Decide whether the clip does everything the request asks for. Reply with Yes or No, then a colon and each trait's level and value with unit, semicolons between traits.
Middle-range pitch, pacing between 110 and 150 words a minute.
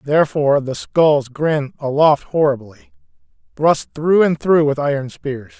Yes: medium, 145 Hz; average, 140 wpm